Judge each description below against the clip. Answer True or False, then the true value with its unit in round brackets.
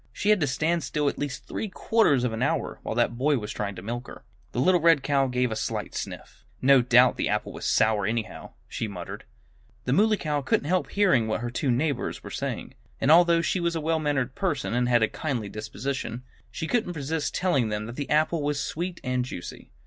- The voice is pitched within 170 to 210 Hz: False (140 Hz)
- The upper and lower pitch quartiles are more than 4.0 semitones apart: True (5.2 semitones)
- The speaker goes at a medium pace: False (225 wpm)